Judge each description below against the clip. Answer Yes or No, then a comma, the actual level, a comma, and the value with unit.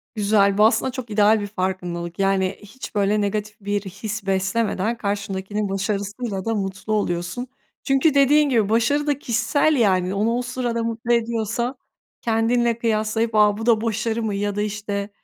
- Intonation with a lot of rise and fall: No, average, 2.7 semitones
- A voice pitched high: Yes, high, 215 Hz